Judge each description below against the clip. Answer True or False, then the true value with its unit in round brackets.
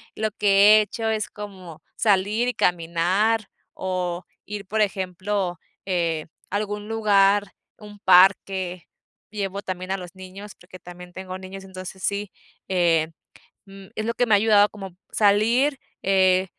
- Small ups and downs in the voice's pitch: True (2.1 semitones)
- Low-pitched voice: False (195 Hz)